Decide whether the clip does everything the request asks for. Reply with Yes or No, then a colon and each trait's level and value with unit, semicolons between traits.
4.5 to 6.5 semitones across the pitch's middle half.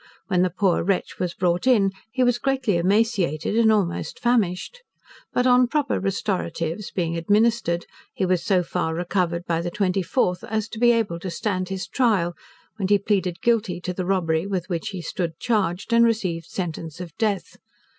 No: average, 4.1 semitones